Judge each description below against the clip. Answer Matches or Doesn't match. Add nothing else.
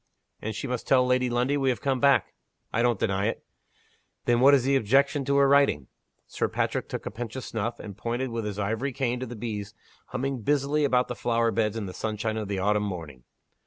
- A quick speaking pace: Matches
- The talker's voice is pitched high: Doesn't match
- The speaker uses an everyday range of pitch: Matches